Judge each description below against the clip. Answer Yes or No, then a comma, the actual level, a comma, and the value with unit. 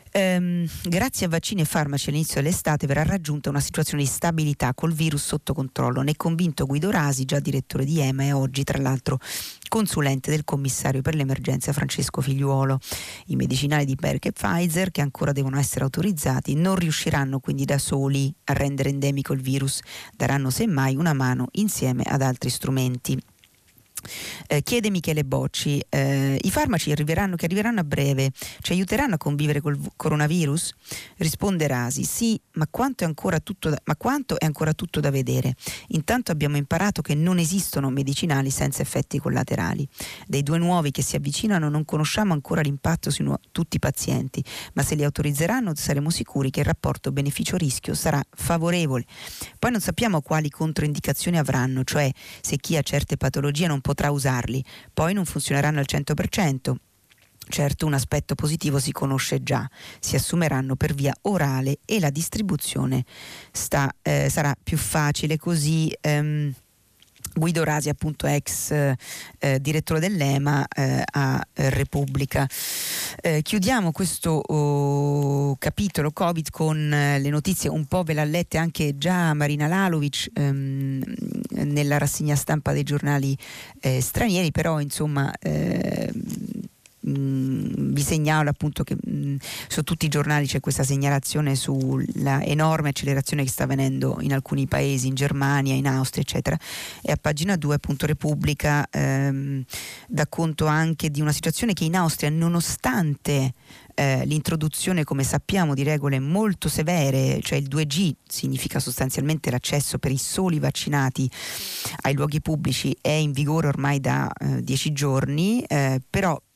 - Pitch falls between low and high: Yes, medium, 145 Hz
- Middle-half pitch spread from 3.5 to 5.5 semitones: No, average, 2.9 semitones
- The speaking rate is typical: Yes, average, 150 wpm